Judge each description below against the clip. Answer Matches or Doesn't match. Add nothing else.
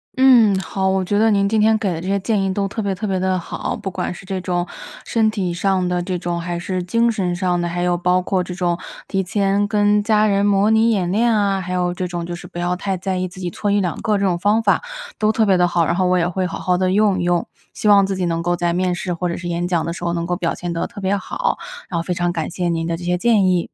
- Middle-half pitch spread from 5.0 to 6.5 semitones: Doesn't match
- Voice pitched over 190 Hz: Doesn't match